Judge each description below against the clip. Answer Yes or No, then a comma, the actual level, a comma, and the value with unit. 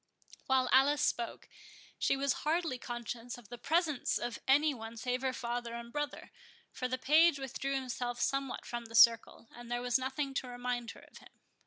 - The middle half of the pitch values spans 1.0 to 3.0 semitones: Yes, narrow, 2.4 semitones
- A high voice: Yes, very high, 255 Hz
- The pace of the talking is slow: No, average, 185 wpm